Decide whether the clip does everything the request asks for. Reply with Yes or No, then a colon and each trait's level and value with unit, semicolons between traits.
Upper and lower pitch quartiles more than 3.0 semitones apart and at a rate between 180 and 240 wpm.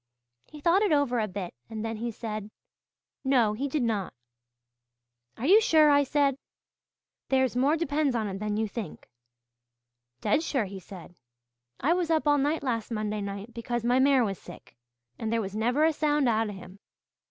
Yes: average, 5.3 semitones; average, 185 wpm